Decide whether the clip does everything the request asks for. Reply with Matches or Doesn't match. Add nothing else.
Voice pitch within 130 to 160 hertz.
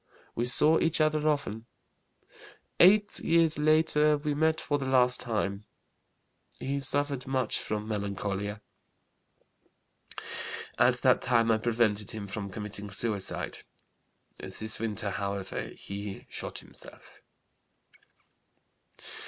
Doesn't match